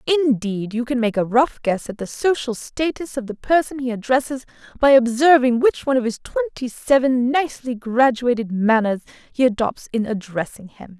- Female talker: Yes, female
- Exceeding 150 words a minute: Yes, average, 175 wpm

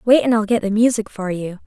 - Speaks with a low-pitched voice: No, high, 215 Hz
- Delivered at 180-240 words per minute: No, fast, 290 wpm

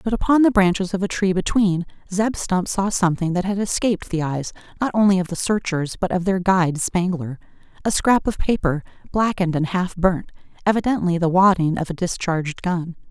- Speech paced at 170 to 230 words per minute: Yes, average, 185 wpm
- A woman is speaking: Yes, female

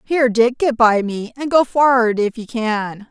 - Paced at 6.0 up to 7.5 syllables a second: No, 4.4 syllables/s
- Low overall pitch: No, high, 235 Hz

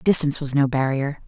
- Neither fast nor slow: Yes, average, 190 wpm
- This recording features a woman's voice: Yes, female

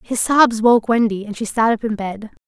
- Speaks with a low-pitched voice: No, high, 225 Hz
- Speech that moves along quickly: Yes, fast, 245 wpm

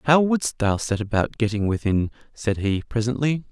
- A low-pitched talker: Yes, low, 115 Hz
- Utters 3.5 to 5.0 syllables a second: Yes, 4.9 syllables/s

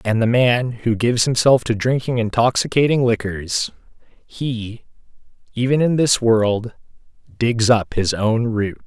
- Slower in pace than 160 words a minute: Yes, slow, 135 wpm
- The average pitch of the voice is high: No, low, 115 Hz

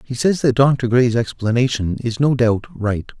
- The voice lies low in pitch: Yes, low, 120 Hz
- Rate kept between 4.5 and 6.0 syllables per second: No, 4.3 syllables/s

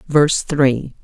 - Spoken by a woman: Yes, female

